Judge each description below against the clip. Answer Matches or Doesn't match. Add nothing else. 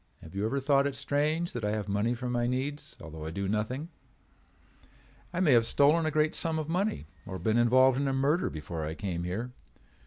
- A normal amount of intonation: Doesn't match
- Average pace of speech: Doesn't match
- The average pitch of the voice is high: Doesn't match